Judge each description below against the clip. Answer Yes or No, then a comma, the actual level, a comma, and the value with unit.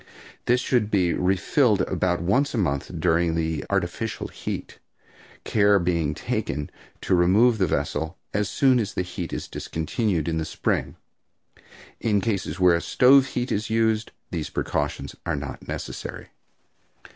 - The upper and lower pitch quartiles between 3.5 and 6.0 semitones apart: Yes, average, 4.9 semitones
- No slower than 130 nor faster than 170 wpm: Yes, average, 140 wpm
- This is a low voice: Yes, very low, 95 Hz